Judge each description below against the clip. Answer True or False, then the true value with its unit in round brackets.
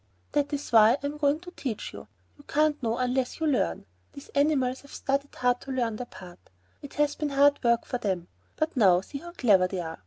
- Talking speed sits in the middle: False (225 wpm)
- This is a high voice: True (265 Hz)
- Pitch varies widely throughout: False (4.2 semitones)